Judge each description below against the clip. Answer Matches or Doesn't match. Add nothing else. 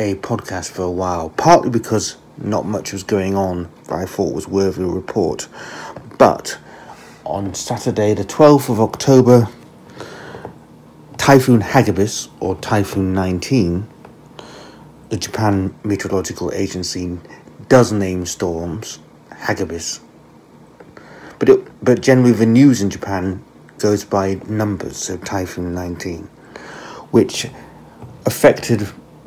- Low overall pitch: Matches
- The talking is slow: Matches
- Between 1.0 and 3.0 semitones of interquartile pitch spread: Doesn't match